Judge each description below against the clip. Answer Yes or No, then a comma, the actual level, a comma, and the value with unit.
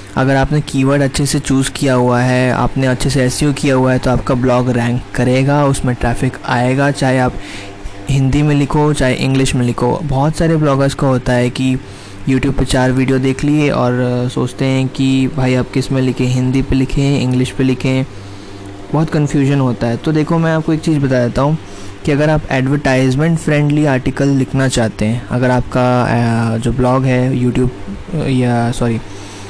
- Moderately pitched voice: No, low, 130 Hz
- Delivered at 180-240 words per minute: Yes, average, 185 wpm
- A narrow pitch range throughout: Yes, narrow, 2.0 semitones